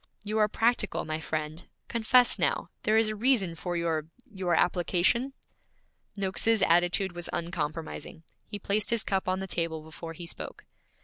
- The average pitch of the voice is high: No, medium, 180 Hz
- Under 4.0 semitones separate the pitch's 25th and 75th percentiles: No, average, 4.3 semitones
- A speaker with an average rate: Yes, average, 160 wpm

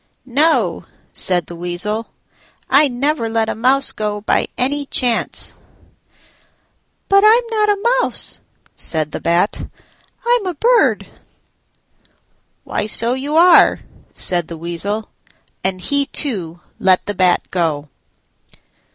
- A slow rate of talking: Yes, slow, 120 wpm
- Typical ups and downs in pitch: No, wide, 8.5 semitones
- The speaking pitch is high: Yes, high, 225 Hz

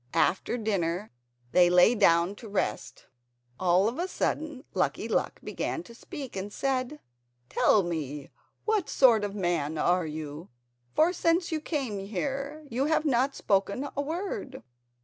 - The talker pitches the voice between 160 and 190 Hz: No, high, 225 Hz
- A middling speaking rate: Yes, average, 150 wpm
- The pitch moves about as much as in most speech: No, wide, 8.1 semitones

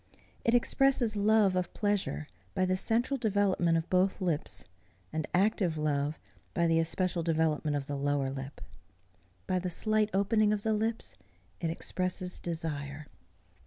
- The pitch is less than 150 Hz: No, medium, 180 Hz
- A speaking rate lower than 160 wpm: Yes, average, 145 wpm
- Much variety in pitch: No, average, 4.9 semitones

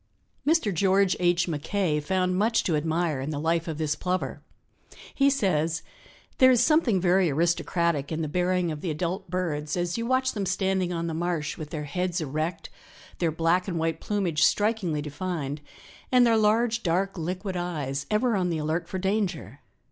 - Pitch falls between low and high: Yes, medium, 175 Hz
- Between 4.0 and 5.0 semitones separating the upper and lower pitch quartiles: No, average, 3.5 semitones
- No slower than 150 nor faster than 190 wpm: Yes, average, 180 wpm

